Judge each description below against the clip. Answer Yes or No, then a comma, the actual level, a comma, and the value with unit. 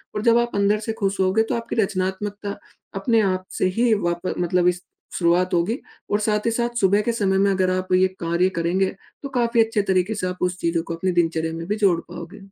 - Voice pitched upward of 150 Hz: Yes, high, 190 Hz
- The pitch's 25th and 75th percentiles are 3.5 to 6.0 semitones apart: No, average, 3.1 semitones